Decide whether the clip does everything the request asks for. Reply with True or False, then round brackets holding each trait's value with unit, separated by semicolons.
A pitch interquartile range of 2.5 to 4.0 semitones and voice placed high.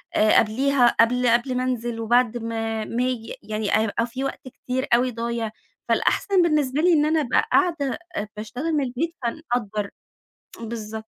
True (3.3 semitones; 245 Hz)